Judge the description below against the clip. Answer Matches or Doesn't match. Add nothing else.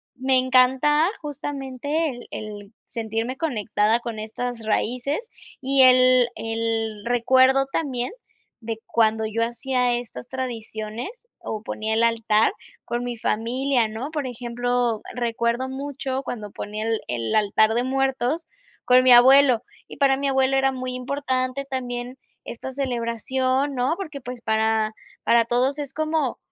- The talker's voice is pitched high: Matches